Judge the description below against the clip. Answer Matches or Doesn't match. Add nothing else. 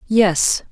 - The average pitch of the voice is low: Doesn't match